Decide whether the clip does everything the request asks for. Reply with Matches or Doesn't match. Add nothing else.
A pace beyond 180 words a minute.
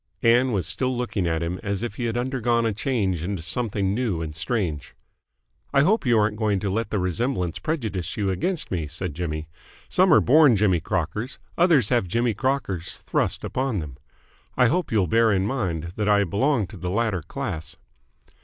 Matches